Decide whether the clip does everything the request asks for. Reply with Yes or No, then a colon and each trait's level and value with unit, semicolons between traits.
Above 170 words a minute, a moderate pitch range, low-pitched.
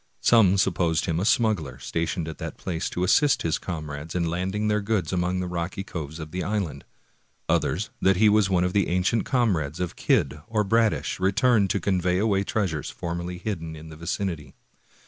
Yes: average, 185 wpm; average, 3.6 semitones; very low, 90 Hz